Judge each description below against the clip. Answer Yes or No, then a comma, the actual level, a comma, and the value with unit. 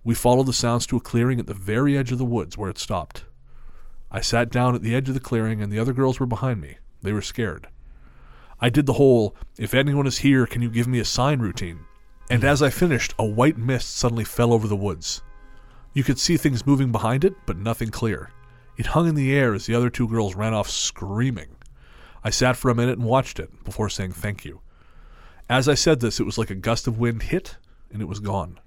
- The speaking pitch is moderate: No, low, 115 Hz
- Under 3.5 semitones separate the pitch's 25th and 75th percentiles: No, average, 3.8 semitones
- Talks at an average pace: No, fast, 240 wpm